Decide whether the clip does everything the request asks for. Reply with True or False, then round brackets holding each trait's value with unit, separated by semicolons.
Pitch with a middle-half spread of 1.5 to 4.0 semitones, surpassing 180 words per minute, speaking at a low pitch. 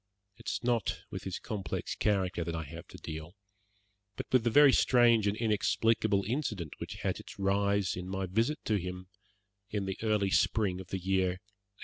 True (3.3 semitones; 190 wpm; 100 Hz)